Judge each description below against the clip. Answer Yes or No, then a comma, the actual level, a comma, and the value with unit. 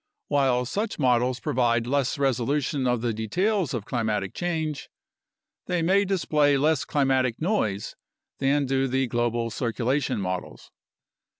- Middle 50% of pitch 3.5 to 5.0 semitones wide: Yes, average, 3.8 semitones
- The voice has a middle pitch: No, low, 130 Hz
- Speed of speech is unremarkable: No, slow, 125 wpm